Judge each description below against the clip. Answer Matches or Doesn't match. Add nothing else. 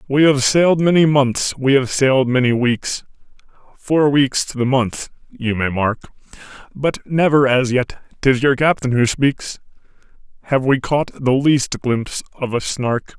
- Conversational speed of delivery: Matches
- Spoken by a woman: Doesn't match